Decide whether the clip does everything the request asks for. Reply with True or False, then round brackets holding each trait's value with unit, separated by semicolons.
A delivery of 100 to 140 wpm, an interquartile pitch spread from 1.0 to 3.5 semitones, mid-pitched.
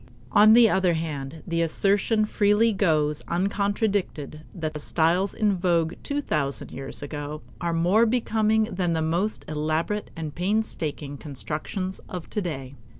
False (135 wpm; 5.1 semitones; 175 Hz)